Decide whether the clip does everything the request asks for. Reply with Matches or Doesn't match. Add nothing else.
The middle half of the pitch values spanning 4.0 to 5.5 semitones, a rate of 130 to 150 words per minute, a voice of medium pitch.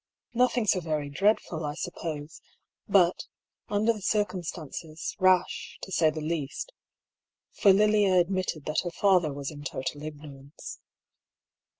Matches